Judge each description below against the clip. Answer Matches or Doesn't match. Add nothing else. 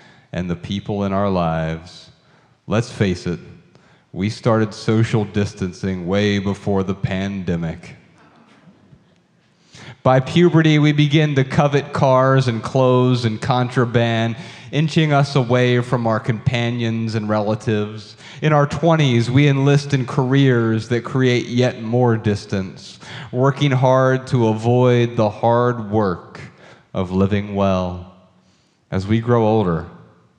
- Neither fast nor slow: Doesn't match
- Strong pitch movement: Doesn't match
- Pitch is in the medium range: Doesn't match